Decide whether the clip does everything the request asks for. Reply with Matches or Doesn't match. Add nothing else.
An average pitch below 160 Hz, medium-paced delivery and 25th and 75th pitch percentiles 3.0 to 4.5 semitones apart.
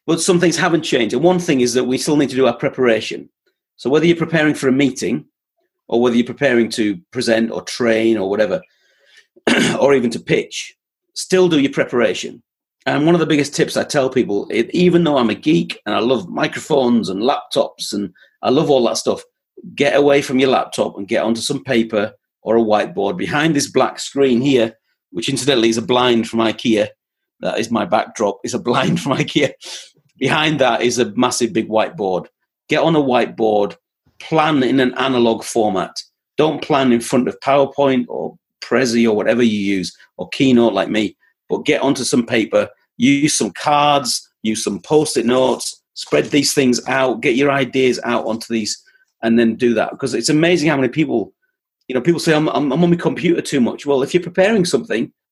Doesn't match